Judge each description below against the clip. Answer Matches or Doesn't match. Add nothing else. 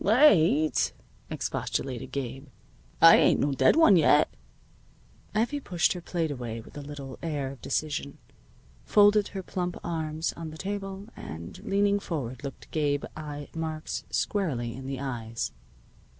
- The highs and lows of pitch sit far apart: Matches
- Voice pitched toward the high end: Doesn't match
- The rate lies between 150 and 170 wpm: Doesn't match